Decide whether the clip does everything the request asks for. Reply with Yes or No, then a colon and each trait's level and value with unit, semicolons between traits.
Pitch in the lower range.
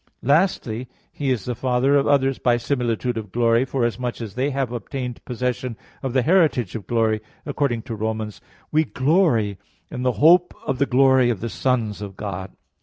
Yes: low, 125 Hz